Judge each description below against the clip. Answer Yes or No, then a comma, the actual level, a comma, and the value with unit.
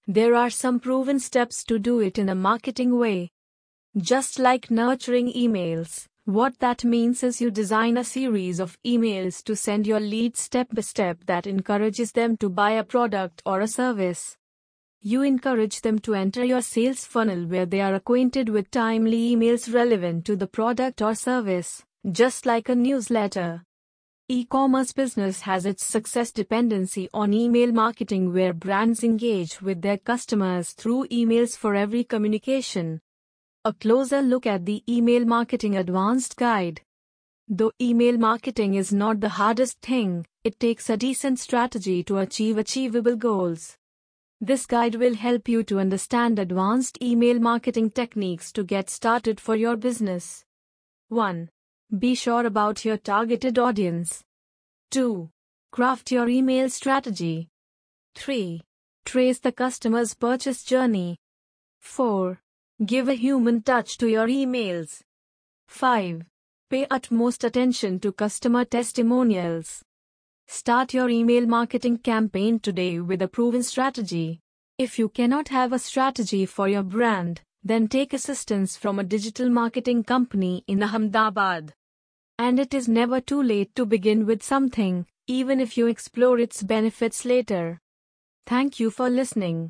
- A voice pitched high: Yes, high, 225 Hz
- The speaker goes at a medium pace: Yes, average, 145 wpm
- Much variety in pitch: No, average, 3.9 semitones